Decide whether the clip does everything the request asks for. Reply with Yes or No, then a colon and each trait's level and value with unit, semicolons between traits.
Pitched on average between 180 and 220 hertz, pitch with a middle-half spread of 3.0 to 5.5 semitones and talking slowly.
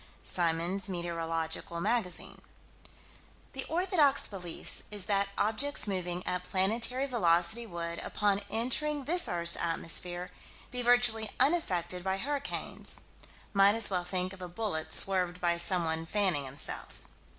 Yes: high, 190 Hz; average, 4.9 semitones; slow, 115 wpm